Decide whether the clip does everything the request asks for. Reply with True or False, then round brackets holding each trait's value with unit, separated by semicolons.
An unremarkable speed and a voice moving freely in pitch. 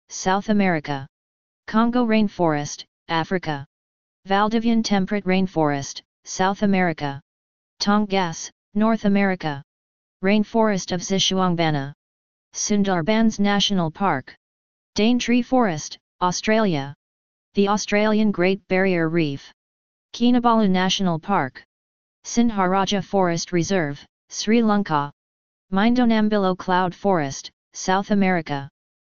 False (85 wpm; 5.9 semitones)